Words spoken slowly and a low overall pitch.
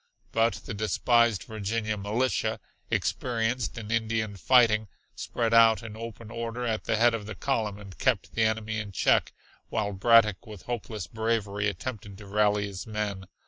No: average, 160 wpm; low, 110 Hz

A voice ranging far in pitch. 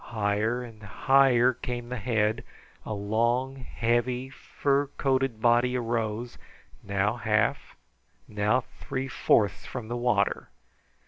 No: average, 2.8 semitones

